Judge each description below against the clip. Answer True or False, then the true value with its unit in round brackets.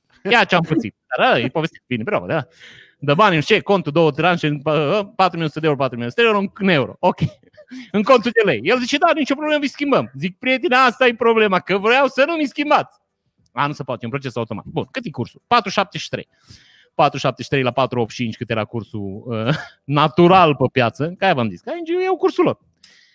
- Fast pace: True (215 wpm)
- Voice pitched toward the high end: False (180 Hz)